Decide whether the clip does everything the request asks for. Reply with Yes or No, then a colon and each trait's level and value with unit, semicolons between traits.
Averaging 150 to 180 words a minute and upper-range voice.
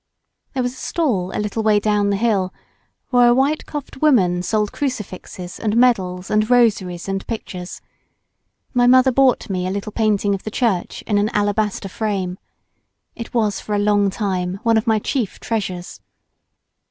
Yes: average, 170 wpm; high, 210 Hz